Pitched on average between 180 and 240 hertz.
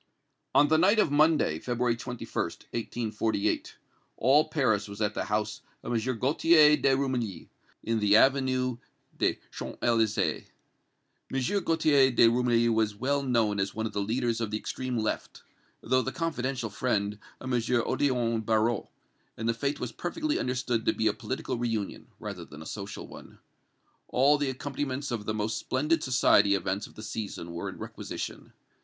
No: low, 120 Hz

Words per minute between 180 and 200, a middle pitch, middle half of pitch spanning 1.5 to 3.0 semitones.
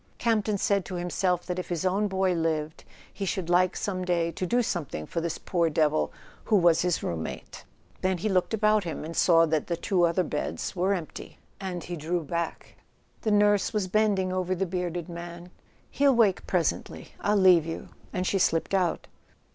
Yes: average, 185 wpm; medium, 180 Hz; narrow, 2.4 semitones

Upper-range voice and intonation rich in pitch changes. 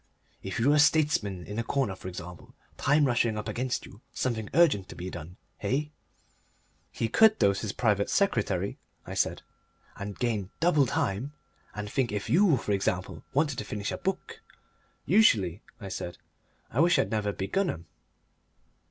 No: low, 110 Hz; wide, 6.6 semitones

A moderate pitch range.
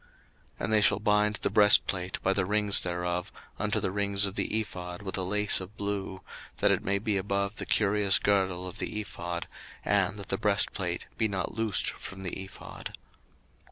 No: narrow, 2.0 semitones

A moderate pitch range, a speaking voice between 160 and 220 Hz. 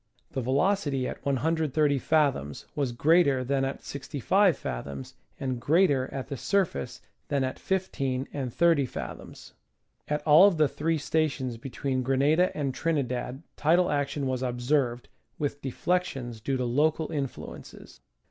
No: average, 3.5 semitones; medium, 140 Hz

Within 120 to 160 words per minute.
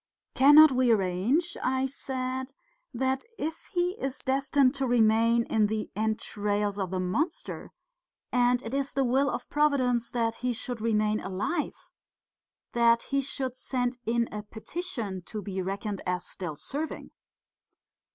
Yes: average, 140 wpm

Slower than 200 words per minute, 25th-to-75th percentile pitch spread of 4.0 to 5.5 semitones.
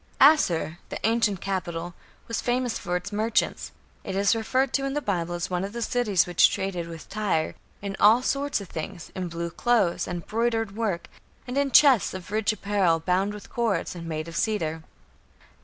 Yes: average, 190 wpm; average, 4.8 semitones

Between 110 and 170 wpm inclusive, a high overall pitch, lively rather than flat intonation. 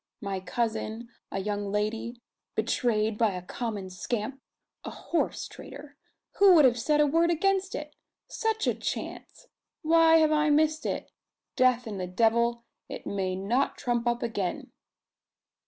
Yes: average, 150 wpm; high, 235 Hz; wide, 6.1 semitones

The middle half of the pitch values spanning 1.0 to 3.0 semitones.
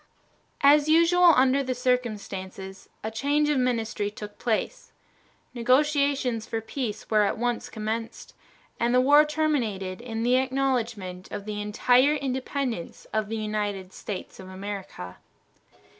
No: average, 4.4 semitones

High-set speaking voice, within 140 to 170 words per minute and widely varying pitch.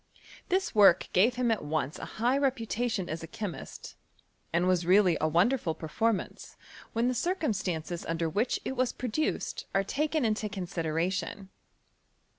Yes: high, 205 Hz; average, 150 wpm; wide, 6.3 semitones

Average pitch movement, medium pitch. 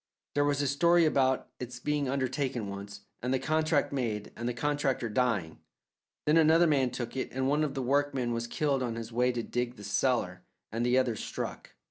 No: average, 3.4 semitones; low, 130 Hz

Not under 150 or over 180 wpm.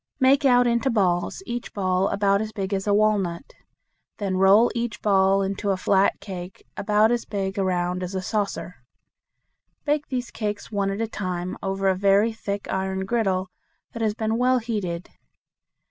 Yes: average, 170 wpm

